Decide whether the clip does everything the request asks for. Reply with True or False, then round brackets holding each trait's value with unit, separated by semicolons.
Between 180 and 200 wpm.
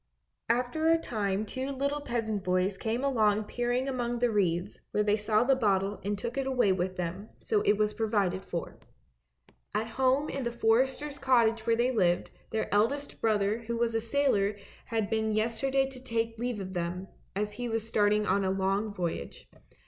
True (185 wpm)